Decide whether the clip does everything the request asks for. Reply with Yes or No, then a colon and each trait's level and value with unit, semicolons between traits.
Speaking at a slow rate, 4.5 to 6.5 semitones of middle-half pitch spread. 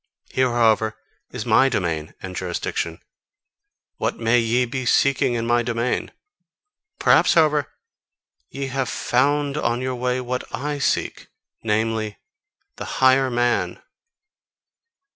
No: slow, 120 wpm; average, 2.9 semitones